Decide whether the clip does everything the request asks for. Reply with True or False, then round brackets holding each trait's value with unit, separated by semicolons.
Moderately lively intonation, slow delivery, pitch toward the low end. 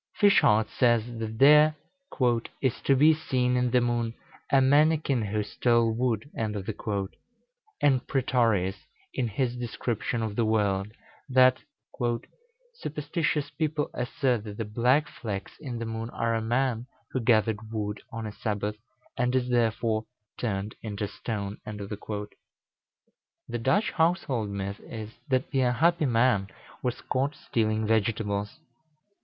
True (3.5 semitones; 130 wpm; 115 Hz)